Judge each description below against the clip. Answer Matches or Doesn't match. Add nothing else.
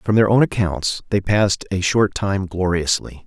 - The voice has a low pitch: Matches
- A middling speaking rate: Matches